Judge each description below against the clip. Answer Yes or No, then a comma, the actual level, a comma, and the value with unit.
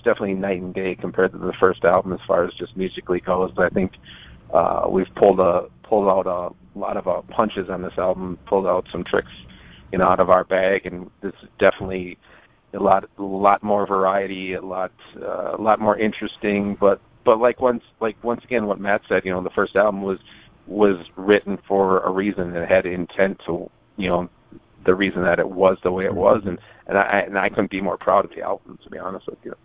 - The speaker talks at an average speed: No, fast, 225 wpm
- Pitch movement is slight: Yes, narrow, 1.7 semitones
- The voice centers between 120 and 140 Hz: No, very low, 95 Hz